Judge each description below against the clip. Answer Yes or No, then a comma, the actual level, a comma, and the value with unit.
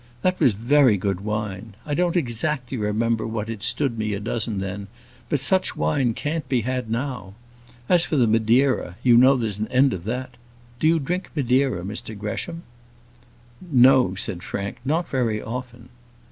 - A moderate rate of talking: Yes, average, 170 wpm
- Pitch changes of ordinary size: Yes, average, 4.3 semitones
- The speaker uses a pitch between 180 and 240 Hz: No, low, 120 Hz